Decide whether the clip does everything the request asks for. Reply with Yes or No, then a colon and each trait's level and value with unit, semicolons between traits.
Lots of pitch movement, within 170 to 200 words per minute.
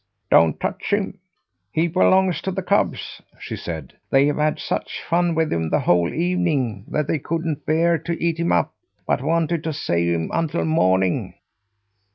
Yes: wide, 8.8 semitones; average, 175 wpm